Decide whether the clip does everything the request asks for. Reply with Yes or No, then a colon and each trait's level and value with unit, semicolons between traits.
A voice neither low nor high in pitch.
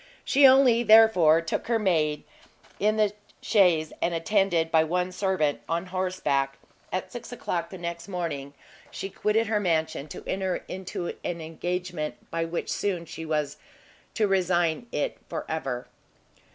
Yes: medium, 175 Hz